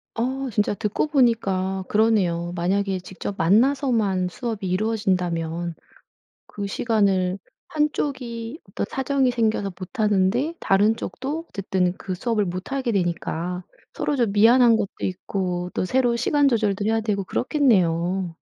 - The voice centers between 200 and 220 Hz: Yes, high, 205 Hz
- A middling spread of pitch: Yes, average, 4.6 semitones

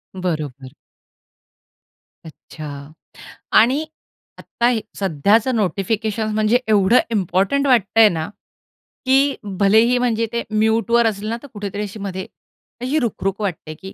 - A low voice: No, high, 215 Hz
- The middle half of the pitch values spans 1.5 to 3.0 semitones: No, average, 3.7 semitones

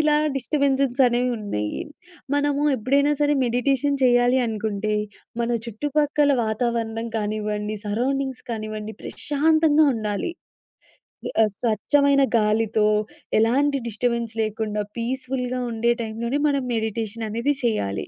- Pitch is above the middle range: Yes, high, 235 Hz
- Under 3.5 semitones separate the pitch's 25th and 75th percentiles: No, average, 4.2 semitones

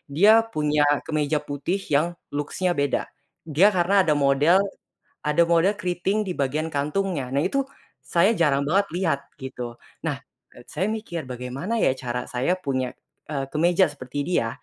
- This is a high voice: No, medium, 150 Hz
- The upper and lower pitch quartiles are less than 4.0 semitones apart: No, average, 4.8 semitones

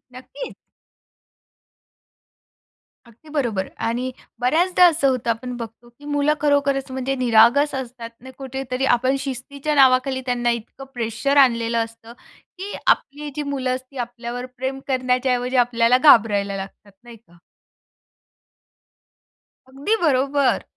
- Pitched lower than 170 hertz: No, very high, 255 Hz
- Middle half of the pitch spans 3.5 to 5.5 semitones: No, average, 2.8 semitones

